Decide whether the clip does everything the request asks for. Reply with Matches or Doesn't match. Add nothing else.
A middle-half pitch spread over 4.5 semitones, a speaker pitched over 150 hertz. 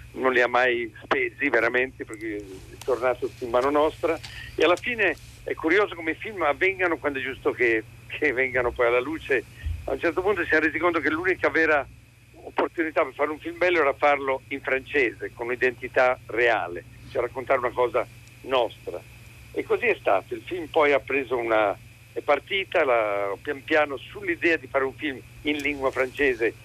Doesn't match